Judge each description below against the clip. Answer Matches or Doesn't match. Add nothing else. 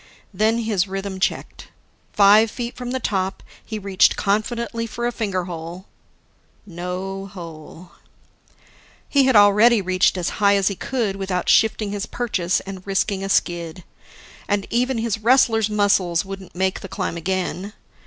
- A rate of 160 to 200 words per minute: Doesn't match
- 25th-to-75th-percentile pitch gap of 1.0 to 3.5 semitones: Matches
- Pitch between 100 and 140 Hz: Doesn't match